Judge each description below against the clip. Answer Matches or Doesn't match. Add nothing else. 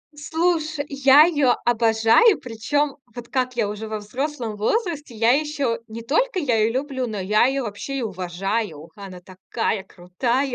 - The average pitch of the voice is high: Matches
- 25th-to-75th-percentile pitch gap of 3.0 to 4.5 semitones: Doesn't match